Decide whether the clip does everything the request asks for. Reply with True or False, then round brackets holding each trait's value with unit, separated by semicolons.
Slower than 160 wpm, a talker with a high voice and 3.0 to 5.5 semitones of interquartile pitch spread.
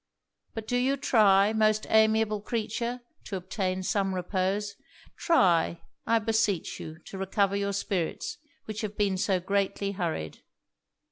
False (135 wpm; 200 Hz; 2.5 semitones)